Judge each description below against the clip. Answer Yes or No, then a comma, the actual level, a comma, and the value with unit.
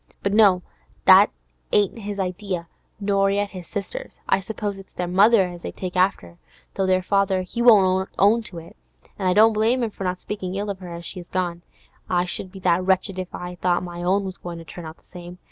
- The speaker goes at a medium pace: No, fast, 225 wpm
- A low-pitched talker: No, medium, 185 Hz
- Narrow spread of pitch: Yes, narrow, 2.1 semitones